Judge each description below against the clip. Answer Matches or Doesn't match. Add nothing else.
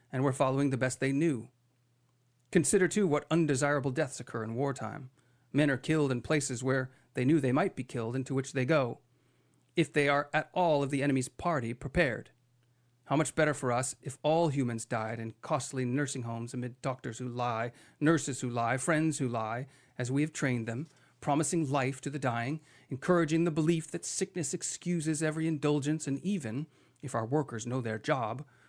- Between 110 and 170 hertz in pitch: Matches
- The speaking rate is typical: Matches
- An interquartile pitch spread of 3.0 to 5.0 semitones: Matches